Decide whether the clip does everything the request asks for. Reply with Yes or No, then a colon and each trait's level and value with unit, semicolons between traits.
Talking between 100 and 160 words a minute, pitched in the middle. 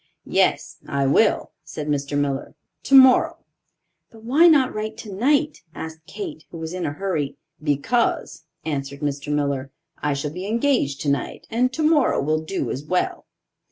Yes: average, 150 wpm; medium, 160 Hz